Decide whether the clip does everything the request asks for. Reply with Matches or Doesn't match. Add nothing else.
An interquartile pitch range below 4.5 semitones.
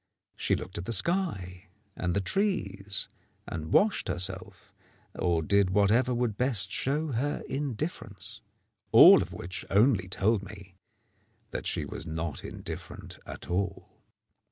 Doesn't match